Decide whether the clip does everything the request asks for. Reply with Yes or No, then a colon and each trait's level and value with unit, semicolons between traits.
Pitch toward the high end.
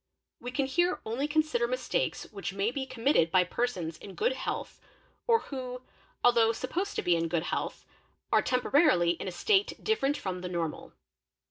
Yes: very high, 250 Hz